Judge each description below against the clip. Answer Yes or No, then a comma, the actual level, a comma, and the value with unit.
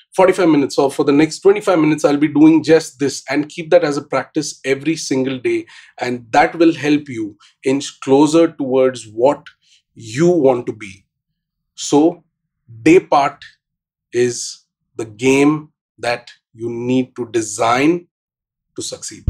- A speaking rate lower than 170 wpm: Yes, average, 150 wpm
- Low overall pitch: No, medium, 150 Hz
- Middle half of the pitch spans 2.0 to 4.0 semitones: No, average, 4.5 semitones